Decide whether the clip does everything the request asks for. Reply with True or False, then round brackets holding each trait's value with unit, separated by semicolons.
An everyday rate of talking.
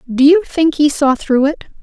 False (230 wpm)